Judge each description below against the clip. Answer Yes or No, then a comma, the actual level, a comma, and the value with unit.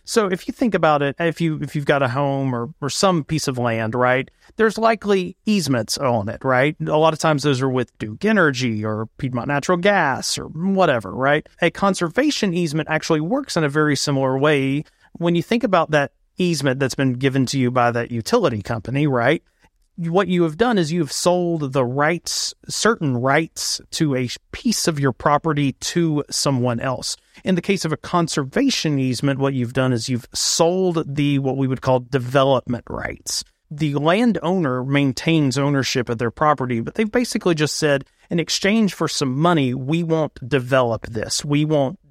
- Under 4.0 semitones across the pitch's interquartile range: No, average, 4.6 semitones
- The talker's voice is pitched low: No, medium, 145 Hz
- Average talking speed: Yes, average, 190 wpm